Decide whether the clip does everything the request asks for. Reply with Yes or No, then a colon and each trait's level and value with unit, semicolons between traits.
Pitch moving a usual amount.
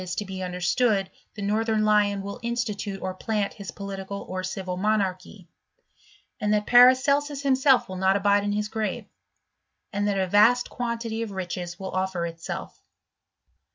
Yes: average, 3.0 semitones